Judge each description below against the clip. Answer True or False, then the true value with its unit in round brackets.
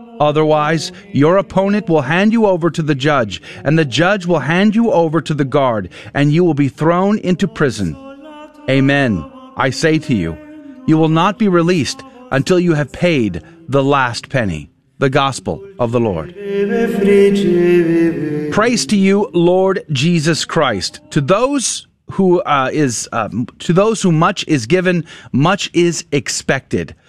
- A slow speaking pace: False (155 wpm)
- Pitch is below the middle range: False (170 Hz)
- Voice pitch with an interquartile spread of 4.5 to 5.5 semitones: True (5.1 semitones)